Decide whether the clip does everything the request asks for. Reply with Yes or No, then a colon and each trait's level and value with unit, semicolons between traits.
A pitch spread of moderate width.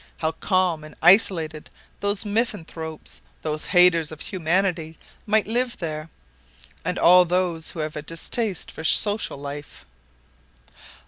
Yes: average, 3.7 semitones